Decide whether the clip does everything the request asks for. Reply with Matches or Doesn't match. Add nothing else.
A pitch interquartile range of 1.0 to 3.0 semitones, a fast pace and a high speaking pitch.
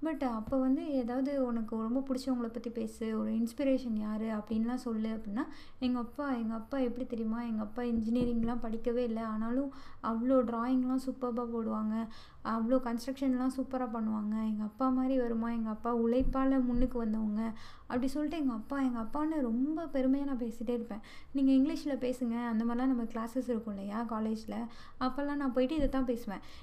Matches